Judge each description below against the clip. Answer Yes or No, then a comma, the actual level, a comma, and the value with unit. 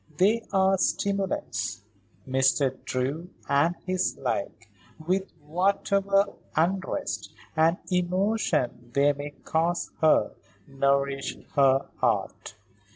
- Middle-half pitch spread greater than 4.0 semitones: Yes, wide, 5.6 semitones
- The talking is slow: Yes, slow, 95 wpm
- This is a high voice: No, medium, 160 Hz